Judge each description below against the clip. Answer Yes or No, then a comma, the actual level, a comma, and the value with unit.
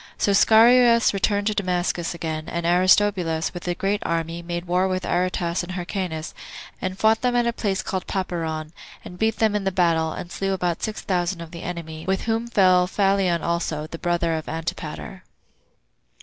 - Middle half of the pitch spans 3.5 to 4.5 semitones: No, average, 2.7 semitones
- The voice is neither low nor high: Yes, medium, 180 Hz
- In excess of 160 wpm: Yes, average, 180 wpm